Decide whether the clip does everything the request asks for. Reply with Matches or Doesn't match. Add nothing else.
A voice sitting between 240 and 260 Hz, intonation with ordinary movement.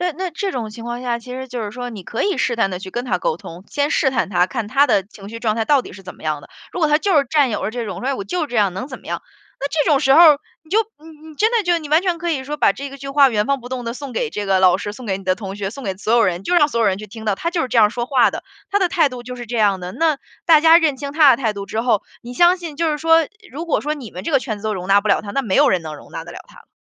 Doesn't match